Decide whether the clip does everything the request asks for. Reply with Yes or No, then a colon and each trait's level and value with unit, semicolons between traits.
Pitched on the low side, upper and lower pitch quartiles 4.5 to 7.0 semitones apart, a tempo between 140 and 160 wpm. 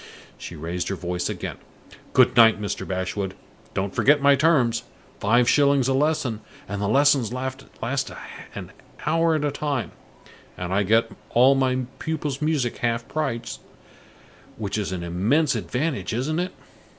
Yes: low, 125 Hz; wide, 5.6 semitones; average, 145 wpm